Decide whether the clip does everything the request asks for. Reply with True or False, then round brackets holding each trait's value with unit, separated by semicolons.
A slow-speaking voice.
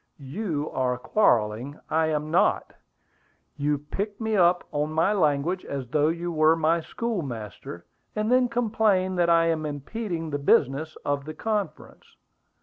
False (145 wpm)